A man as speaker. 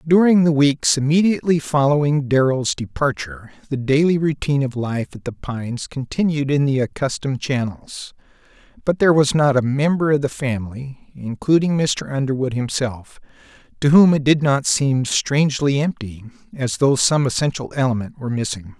Yes: male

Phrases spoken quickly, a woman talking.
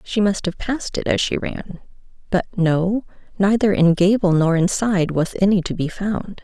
No: average, 175 wpm; female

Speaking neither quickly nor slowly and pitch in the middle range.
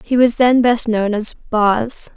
No: average, 195 wpm; high, 230 Hz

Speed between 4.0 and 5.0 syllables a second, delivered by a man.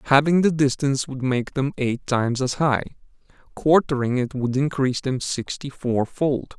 Yes: 4.8 syllables/s; male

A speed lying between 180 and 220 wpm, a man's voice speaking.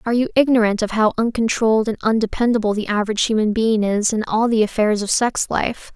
No: average, 200 wpm; female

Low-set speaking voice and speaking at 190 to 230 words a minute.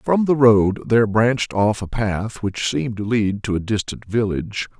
Yes: low, 110 Hz; average, 200 wpm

